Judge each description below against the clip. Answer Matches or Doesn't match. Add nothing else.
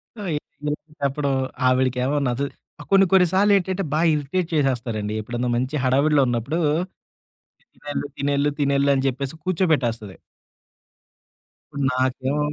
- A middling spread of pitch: Matches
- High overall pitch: Doesn't match